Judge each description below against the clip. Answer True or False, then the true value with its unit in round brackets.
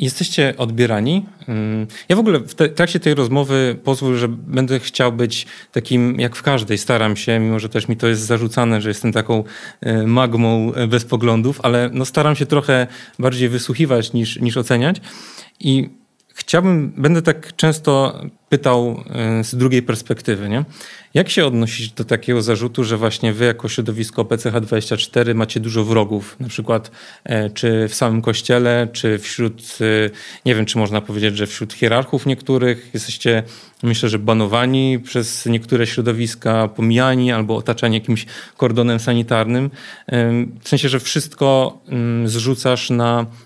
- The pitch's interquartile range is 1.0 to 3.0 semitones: True (2.4 semitones)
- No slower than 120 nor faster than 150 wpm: True (145 wpm)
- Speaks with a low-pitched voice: True (120 Hz)